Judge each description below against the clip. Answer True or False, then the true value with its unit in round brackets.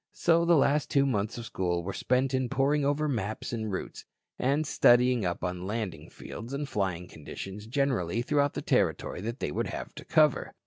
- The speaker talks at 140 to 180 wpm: False (190 wpm)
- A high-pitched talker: False (120 Hz)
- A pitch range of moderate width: False (6.1 semitones)